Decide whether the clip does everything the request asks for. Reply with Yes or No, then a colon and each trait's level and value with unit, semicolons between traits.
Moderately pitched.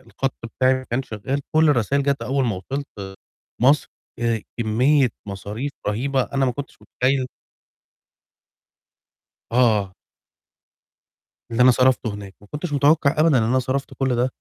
No: low, 130 Hz